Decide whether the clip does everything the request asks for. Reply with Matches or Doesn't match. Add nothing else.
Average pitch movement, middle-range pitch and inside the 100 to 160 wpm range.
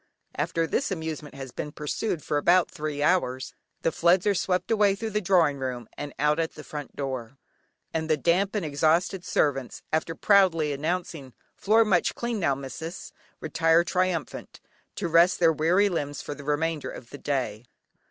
Doesn't match